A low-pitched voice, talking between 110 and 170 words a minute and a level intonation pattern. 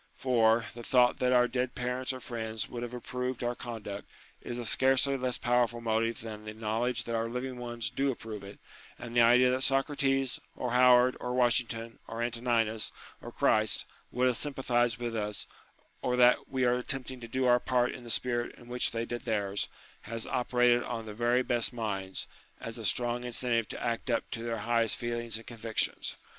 No: low, 120 Hz; average, 195 wpm; narrow, 1.5 semitones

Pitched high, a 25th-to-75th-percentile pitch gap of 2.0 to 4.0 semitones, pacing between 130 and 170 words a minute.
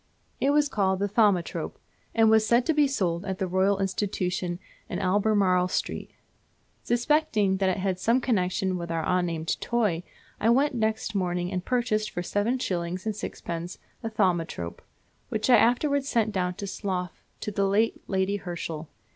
Yes: high, 195 Hz; average, 3.6 semitones; average, 165 wpm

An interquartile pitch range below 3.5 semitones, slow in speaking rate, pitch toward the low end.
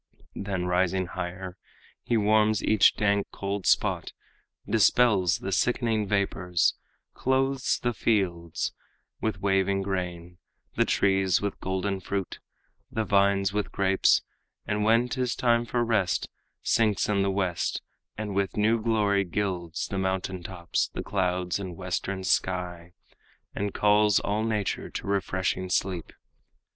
Yes: narrow, 2.4 semitones; slow, 130 wpm; low, 100 Hz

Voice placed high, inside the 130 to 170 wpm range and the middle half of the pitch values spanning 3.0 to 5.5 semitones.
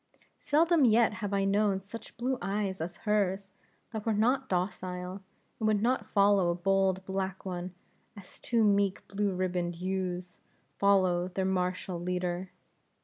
No: high, 195 Hz; average, 145 wpm; narrow, 2.4 semitones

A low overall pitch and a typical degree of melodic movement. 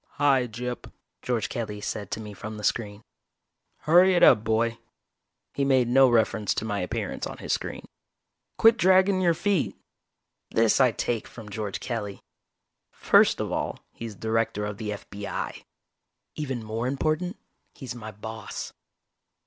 Yes: low, 115 Hz; average, 4.1 semitones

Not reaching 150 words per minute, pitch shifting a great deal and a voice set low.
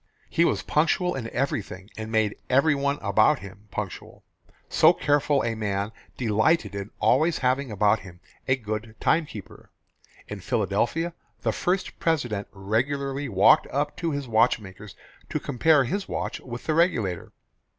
Yes: average, 140 wpm; wide, 5.8 semitones; low, 120 Hz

